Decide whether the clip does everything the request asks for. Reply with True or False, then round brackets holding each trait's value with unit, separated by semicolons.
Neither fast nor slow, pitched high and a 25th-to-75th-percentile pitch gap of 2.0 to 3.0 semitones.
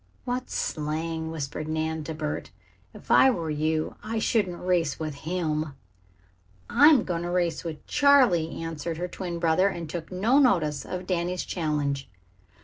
False (150 wpm; 165 Hz; 2.7 semitones)